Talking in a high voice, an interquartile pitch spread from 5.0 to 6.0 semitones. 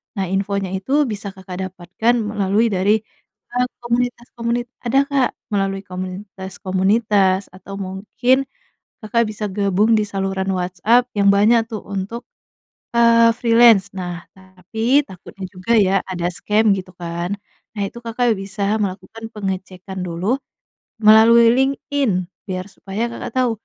No: high, 200 Hz; average, 3.6 semitones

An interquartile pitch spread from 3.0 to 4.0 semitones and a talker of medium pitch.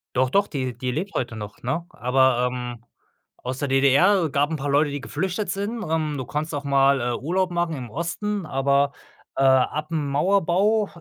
No: average, 4.8 semitones; medium, 145 Hz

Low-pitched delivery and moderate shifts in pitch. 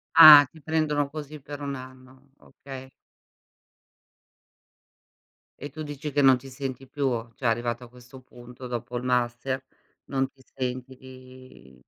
No: low, 130 Hz; narrow, 2.0 semitones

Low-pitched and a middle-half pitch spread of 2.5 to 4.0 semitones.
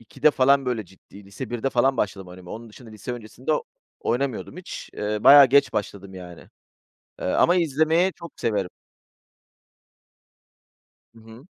No: low, 120 Hz; average, 5.1 semitones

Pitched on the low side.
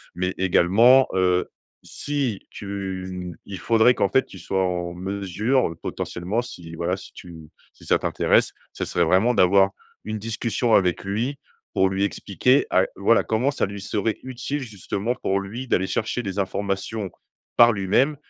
Yes: low, 100 Hz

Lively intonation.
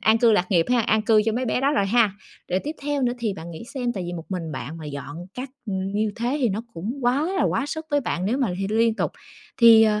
No: average, 4.5 semitones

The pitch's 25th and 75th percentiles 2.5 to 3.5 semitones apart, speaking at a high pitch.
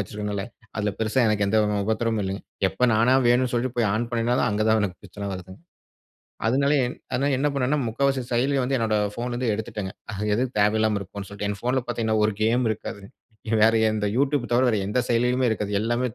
No: average, 3.1 semitones; low, 115 Hz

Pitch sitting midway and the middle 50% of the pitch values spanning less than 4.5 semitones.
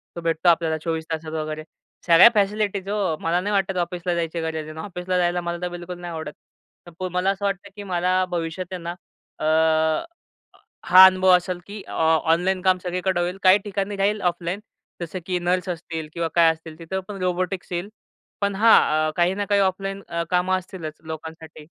Yes: medium, 180 Hz; narrow, 2.4 semitones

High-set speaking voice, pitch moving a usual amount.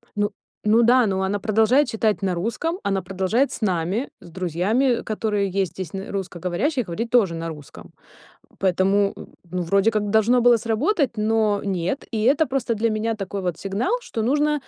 Yes: high, 210 Hz; average, 3.7 semitones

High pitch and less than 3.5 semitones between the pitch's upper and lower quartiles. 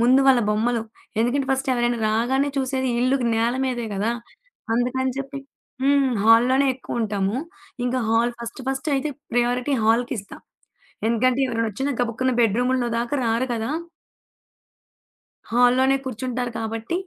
Yes: high, 245 Hz; narrow, 2.4 semitones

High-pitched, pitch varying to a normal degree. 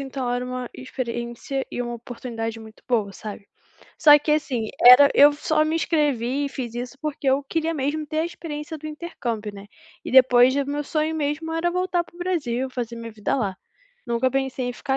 Yes: very high, 265 Hz; average, 4.2 semitones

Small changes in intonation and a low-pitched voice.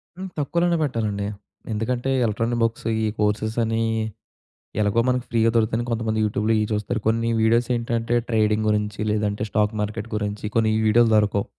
Yes: narrow, 1.7 semitones; low, 110 Hz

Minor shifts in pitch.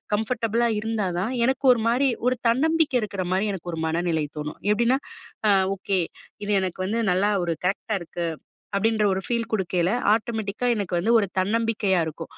No: average, 3.9 semitones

